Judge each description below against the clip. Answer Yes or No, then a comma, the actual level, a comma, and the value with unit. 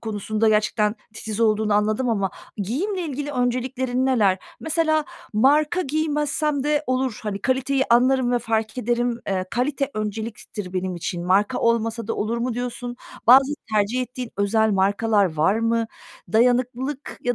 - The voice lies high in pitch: Yes, high, 235 Hz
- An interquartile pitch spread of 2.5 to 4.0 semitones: Yes, average, 3.6 semitones